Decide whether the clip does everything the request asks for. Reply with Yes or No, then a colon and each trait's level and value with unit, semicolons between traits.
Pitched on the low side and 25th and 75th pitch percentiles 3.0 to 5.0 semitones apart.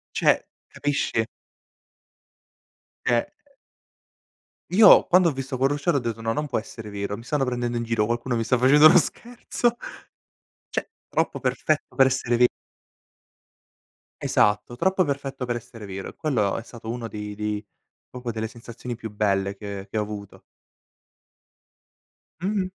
Yes: low, 120 Hz; average, 4.6 semitones